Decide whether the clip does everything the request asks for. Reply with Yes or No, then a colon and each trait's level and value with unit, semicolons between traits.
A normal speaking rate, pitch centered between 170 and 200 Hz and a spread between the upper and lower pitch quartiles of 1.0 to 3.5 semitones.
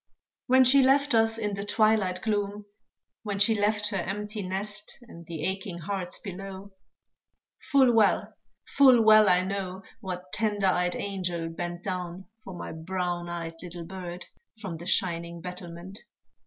Yes: average, 150 wpm; high, 190 Hz; average, 2.9 semitones